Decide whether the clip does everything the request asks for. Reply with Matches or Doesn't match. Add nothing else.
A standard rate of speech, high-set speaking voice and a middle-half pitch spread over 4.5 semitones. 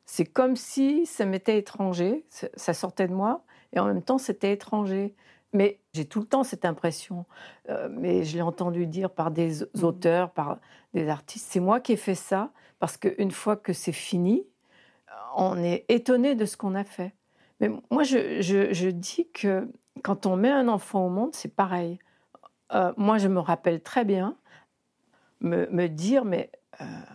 Matches